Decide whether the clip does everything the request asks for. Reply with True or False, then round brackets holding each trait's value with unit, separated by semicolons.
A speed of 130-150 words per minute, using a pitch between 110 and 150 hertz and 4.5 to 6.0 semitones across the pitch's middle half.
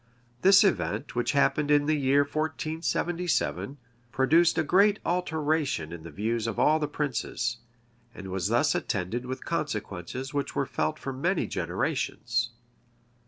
True (135 wpm; 140 Hz; 5.1 semitones)